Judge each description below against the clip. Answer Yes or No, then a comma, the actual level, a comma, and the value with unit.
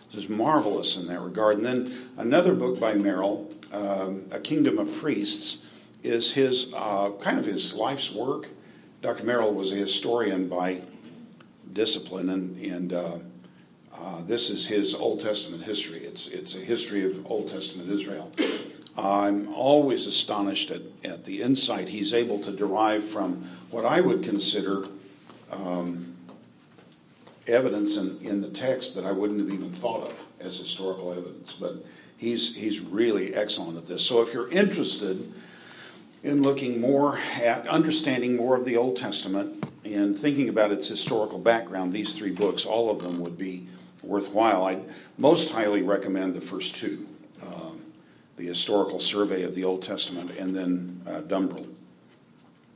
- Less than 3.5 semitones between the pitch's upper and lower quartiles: No, average, 4.2 semitones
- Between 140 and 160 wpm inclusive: Yes, average, 155 wpm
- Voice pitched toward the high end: No, low, 100 Hz